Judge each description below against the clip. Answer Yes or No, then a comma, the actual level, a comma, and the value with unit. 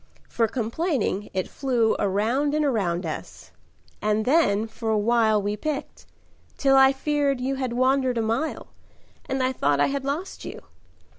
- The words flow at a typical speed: Yes, average, 160 wpm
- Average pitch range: Yes, average, 4.2 semitones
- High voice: Yes, very high, 250 Hz